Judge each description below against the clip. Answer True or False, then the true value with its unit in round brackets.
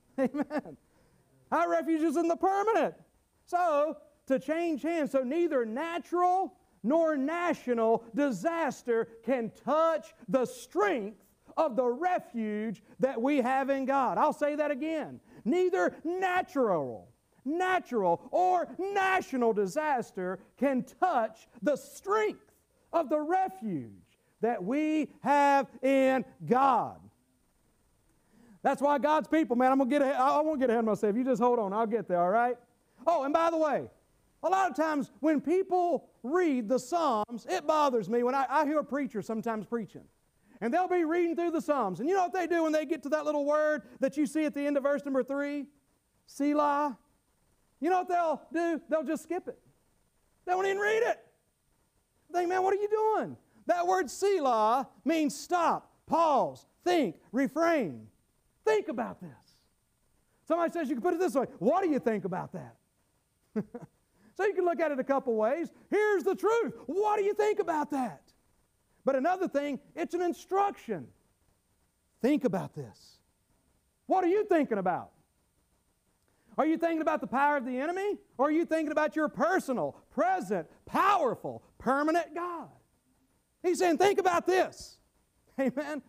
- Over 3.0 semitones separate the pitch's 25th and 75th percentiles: True (5.1 semitones)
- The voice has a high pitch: True (295 Hz)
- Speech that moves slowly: False (160 wpm)